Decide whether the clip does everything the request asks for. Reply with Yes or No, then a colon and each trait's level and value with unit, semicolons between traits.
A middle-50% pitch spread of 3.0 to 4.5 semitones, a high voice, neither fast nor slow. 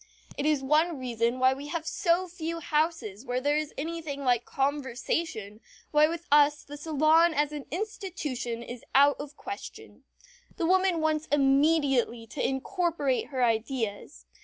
Yes: average, 4.0 semitones; very high, 290 Hz; average, 150 wpm